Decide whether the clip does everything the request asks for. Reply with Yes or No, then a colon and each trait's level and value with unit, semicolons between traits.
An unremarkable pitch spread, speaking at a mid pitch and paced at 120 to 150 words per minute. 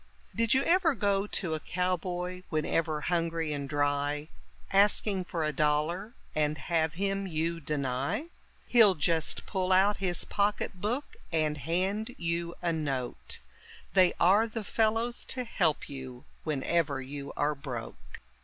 Yes: average, 4.8 semitones; medium, 170 Hz; average, 140 wpm